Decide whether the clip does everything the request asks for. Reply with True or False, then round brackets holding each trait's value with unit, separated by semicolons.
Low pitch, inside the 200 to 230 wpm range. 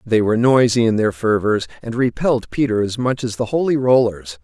True (115 Hz; 205 wpm)